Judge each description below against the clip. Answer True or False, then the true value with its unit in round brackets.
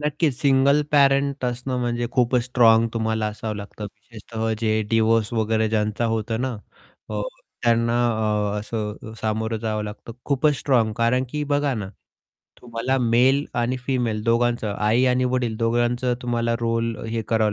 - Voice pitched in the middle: False (115 Hz)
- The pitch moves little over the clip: True (2.2 semitones)